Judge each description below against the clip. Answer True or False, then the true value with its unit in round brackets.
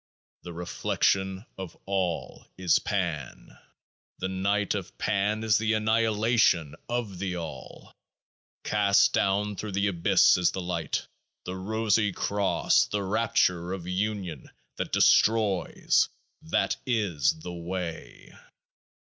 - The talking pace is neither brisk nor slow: False (115 wpm)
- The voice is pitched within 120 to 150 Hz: False (95 Hz)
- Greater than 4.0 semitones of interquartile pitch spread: False (3.1 semitones)